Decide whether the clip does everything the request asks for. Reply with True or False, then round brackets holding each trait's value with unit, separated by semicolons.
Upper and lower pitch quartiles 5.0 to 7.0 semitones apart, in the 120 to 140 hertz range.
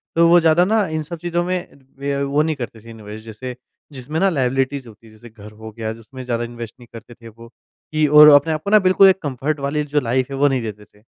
True (5.3 semitones; 135 Hz)